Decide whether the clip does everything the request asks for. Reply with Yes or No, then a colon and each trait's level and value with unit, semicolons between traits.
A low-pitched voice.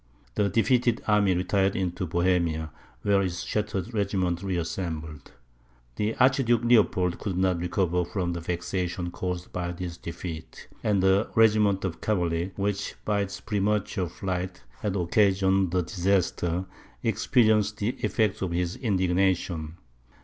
Yes: very low, 95 Hz